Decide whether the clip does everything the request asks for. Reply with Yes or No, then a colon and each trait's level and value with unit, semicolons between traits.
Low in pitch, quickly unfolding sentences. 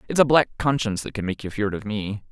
Yes: low, 110 Hz; fast, 285 wpm